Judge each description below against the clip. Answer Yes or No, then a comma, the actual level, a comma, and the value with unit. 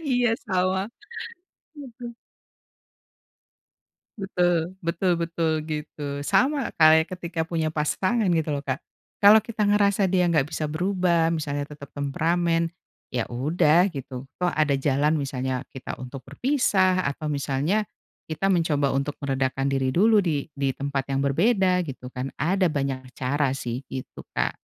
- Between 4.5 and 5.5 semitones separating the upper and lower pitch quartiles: Yes, average, 4.8 semitones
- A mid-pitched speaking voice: Yes, medium, 160 Hz